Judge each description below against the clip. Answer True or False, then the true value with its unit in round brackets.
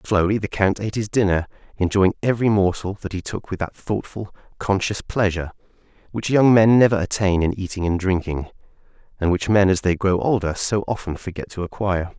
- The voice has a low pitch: True (100 Hz)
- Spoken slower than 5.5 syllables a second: False (5.8 syllables/s)